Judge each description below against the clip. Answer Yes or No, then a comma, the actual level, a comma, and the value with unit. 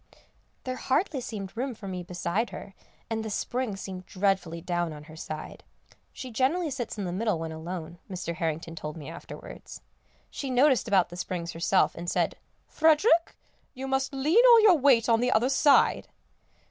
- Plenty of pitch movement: Yes, wide, 7.3 semitones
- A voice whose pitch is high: Yes, high, 205 Hz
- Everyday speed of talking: Yes, average, 175 wpm